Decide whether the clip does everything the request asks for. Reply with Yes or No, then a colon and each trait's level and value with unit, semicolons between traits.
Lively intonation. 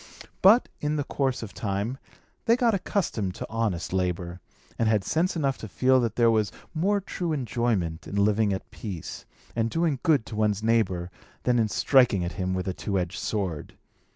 Yes: wide, 6.0 semitones